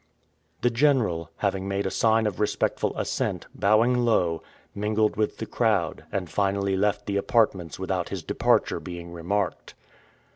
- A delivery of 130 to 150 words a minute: Yes, average, 145 wpm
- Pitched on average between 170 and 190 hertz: No, low, 100 Hz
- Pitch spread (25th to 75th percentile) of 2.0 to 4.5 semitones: Yes, average, 3.3 semitones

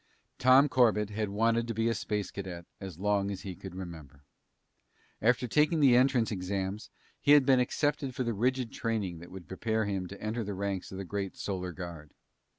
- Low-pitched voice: Yes, low, 105 Hz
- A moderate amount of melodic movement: Yes, average, 4.0 semitones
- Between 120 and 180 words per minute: No, average, 195 wpm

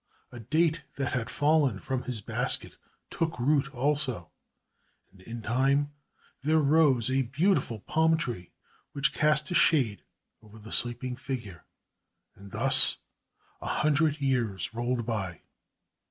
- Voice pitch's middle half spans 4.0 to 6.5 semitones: Yes, average, 4.7 semitones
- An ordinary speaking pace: No, slow, 130 wpm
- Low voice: Yes, low, 130 Hz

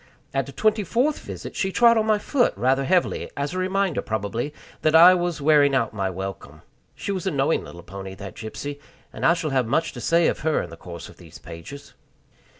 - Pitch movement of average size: No, wide, 9.0 semitones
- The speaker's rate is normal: No, fast, 220 wpm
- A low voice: No, medium, 145 Hz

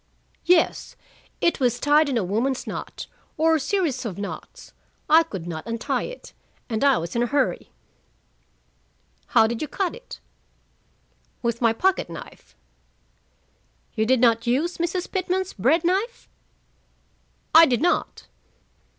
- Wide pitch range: Yes, wide, 6.9 semitones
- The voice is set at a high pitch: Yes, very high, 270 Hz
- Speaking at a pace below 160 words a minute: Yes, slow, 135 wpm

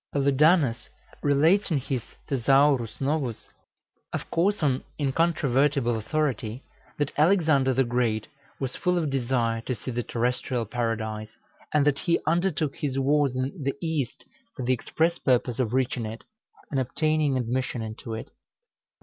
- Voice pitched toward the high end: No, low, 135 Hz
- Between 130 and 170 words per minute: Yes, average, 140 wpm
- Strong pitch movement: No, average, 3.8 semitones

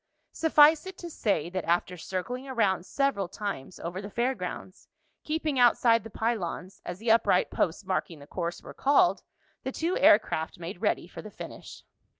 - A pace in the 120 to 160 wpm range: No, average, 175 wpm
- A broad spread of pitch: Yes, wide, 6.8 semitones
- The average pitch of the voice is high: Yes, high, 210 Hz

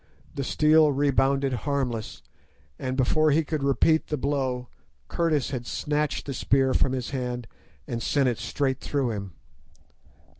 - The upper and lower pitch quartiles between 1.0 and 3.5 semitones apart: Yes, narrow, 2.6 semitones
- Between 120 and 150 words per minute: Yes, average, 145 wpm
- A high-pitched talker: No, low, 135 Hz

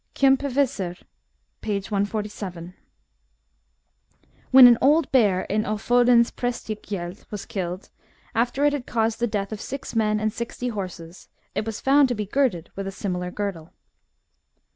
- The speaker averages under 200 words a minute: Yes, average, 140 wpm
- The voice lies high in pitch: Yes, high, 215 Hz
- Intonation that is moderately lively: Yes, average, 3.9 semitones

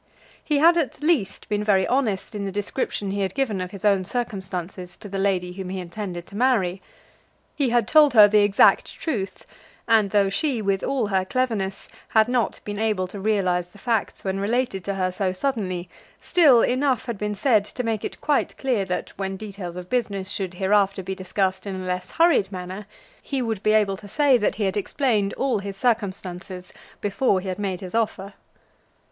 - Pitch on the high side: Yes, high, 200 Hz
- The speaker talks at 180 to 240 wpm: Yes, average, 200 wpm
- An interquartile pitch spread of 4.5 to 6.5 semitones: No, average, 3.4 semitones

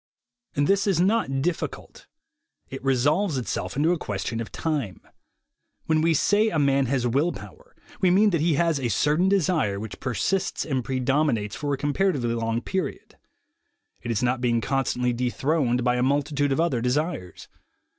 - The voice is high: No, medium, 140 Hz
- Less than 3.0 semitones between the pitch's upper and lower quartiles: No, average, 5.1 semitones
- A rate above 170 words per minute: No, average, 165 wpm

